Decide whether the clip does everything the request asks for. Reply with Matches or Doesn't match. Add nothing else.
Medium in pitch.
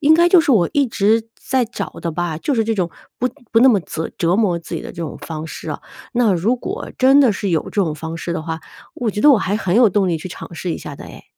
Doesn't match